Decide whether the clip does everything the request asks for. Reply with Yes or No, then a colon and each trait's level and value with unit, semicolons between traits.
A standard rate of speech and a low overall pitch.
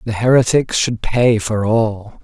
Yes: average, 160 wpm; low, 115 Hz